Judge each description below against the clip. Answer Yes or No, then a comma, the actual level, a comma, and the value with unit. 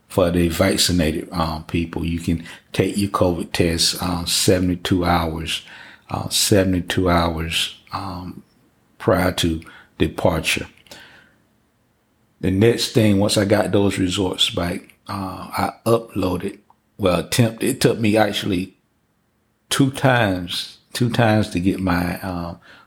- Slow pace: Yes, slow, 125 wpm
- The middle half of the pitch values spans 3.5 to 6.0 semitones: No, average, 3.0 semitones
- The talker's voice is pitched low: Yes, very low, 95 Hz